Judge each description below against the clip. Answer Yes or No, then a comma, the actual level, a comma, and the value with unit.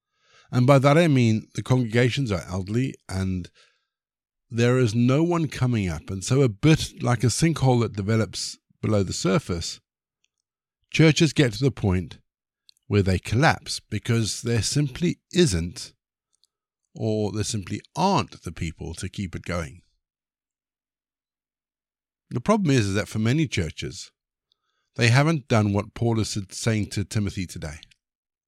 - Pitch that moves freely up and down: Yes, wide, 5.7 semitones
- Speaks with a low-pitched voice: Yes, low, 110 Hz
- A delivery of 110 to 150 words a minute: Yes, average, 145 wpm